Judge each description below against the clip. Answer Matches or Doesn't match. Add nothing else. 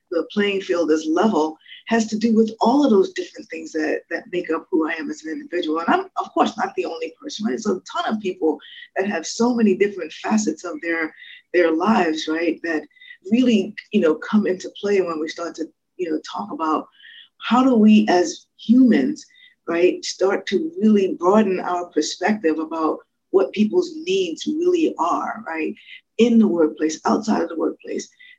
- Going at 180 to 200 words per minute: Matches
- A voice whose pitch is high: Matches